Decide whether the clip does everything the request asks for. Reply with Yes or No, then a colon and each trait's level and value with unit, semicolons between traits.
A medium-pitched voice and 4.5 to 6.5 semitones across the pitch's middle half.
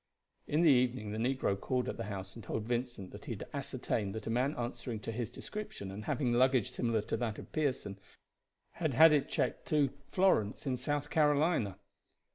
No: low, 125 Hz; average, 4.8 semitones